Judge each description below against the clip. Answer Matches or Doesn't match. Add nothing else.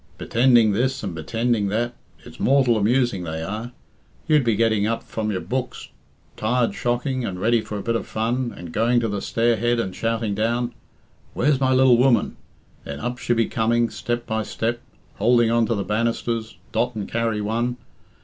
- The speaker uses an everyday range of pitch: Doesn't match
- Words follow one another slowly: Doesn't match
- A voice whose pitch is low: Matches